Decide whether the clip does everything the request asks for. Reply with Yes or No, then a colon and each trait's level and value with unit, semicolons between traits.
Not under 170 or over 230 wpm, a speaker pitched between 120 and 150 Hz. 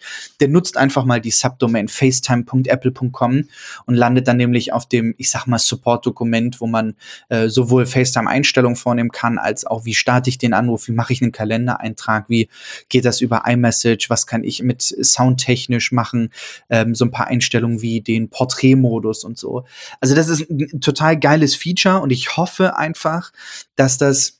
Yes: average, 175 wpm; low, 125 Hz